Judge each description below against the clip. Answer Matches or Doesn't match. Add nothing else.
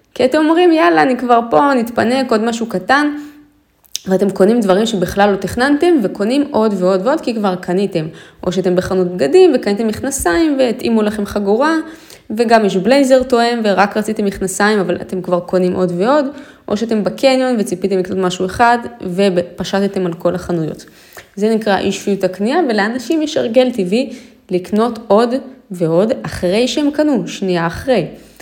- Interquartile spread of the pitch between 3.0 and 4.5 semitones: Doesn't match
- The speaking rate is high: Matches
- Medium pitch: Doesn't match